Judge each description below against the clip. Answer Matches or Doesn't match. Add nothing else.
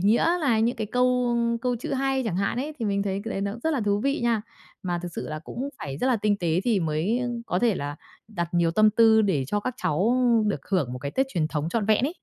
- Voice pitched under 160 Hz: Doesn't match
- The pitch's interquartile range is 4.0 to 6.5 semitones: Matches